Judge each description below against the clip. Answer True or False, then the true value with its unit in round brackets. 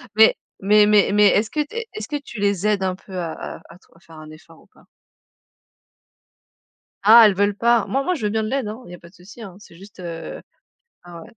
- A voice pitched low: False (205 Hz)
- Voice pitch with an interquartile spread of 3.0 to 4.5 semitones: True (3.7 semitones)